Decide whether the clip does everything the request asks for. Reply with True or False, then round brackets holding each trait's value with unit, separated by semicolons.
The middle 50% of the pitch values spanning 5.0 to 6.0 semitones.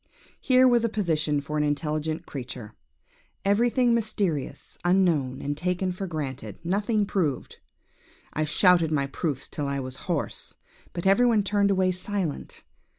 True (5.5 semitones)